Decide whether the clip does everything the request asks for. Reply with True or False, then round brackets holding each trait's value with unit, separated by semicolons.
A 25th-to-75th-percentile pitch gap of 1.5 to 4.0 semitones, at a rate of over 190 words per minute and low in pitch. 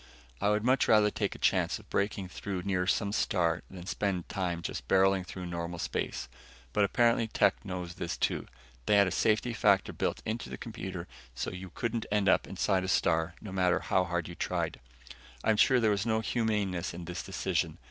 True (3.0 semitones; 200 wpm; 95 Hz)